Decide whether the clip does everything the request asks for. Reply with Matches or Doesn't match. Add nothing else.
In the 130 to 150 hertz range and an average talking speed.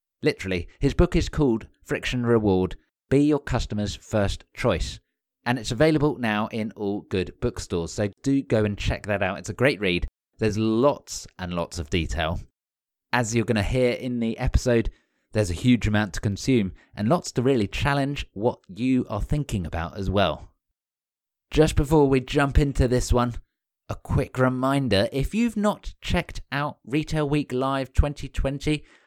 Doesn't match